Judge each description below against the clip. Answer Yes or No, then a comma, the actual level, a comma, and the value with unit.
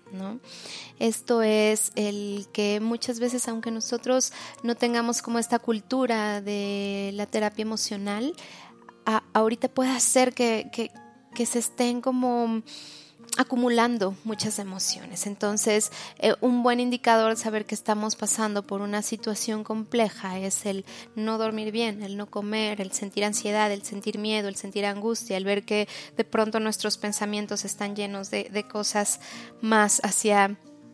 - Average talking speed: Yes, average, 145 wpm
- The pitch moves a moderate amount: No, narrow, 2.2 semitones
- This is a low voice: No, high, 215 Hz